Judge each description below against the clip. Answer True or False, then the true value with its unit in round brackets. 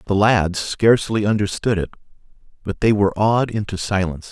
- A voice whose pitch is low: True (100 Hz)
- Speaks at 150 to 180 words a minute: True (155 wpm)